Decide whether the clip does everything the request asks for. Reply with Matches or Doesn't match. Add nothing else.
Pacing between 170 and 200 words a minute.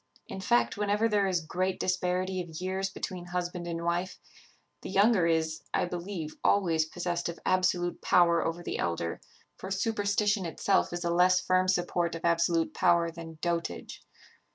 Doesn't match